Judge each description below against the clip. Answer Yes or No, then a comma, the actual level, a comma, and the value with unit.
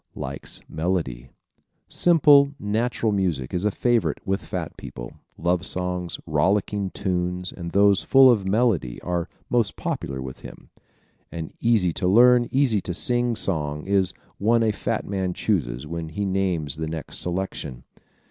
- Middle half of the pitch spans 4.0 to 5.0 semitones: Yes, average, 4.7 semitones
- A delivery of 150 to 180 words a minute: Yes, average, 155 wpm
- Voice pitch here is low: Yes, very low, 95 Hz